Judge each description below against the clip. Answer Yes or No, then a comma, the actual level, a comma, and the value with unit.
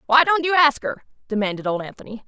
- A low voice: No, very high, 255 Hz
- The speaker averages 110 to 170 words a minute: No, fast, 210 wpm